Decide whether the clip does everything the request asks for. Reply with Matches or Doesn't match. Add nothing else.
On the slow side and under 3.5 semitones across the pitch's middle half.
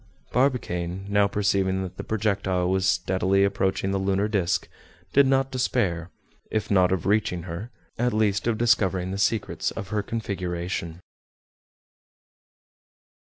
Matches